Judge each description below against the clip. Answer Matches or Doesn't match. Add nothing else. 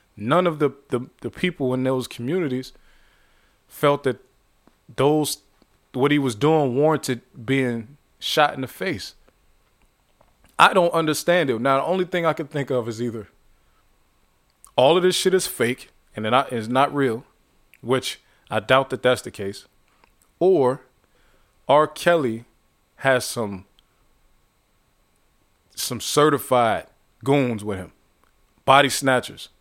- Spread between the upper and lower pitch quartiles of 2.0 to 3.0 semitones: Doesn't match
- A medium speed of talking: Doesn't match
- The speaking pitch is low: Matches